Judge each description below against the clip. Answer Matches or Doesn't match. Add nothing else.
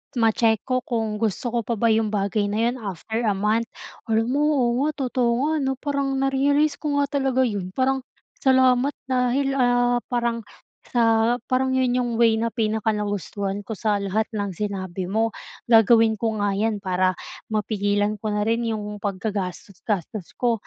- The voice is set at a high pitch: Matches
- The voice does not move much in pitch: Doesn't match